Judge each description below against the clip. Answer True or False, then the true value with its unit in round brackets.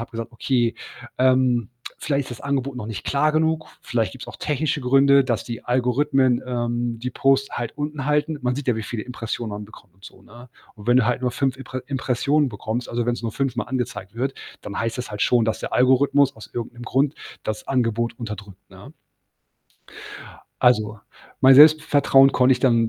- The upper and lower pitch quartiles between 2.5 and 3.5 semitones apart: True (2.9 semitones)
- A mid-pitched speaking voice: False (125 Hz)